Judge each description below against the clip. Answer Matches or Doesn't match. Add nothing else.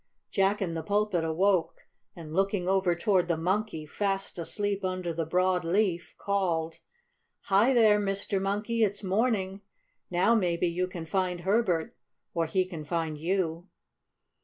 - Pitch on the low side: Doesn't match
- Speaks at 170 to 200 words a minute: Doesn't match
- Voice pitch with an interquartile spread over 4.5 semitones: Doesn't match